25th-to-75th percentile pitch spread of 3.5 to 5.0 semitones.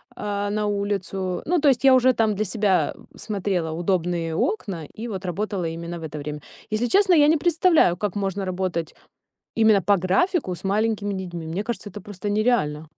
Yes: average, 3.9 semitones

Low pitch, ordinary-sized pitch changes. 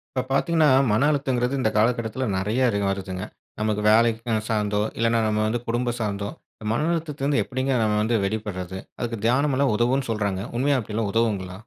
Yes: low, 115 Hz; average, 3.7 semitones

